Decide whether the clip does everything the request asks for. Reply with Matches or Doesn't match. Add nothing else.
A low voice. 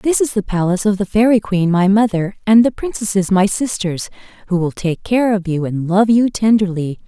Doesn't match